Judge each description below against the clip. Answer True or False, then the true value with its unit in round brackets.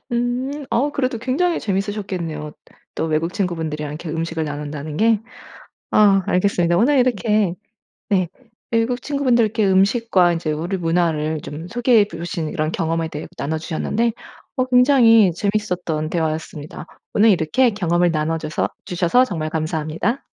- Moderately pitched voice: True (180 Hz)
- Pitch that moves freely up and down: True (6.1 semitones)